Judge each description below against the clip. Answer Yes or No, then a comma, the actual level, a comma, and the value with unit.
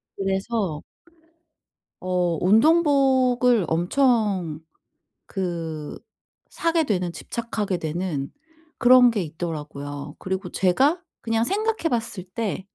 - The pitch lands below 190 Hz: No, high, 195 Hz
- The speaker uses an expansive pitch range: Yes, wide, 6.2 semitones